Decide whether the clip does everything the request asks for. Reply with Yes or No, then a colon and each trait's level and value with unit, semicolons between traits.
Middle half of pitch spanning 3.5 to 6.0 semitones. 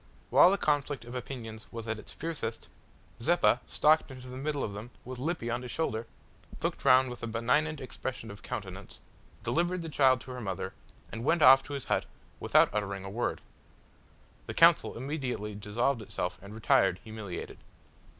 Yes: average, 4.2 semitones